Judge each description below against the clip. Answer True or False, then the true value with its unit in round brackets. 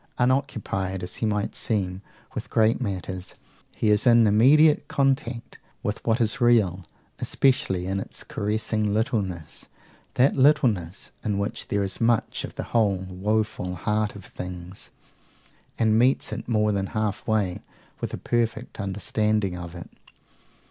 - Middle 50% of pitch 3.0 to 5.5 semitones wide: True (3.4 semitones)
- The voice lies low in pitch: True (105 Hz)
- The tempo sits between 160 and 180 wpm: False (140 wpm)